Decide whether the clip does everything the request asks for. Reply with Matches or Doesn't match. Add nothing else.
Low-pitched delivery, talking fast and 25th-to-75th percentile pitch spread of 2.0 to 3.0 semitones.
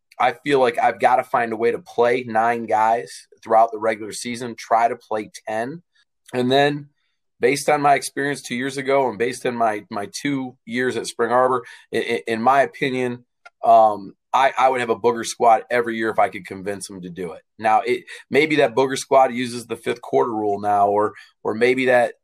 Doesn't match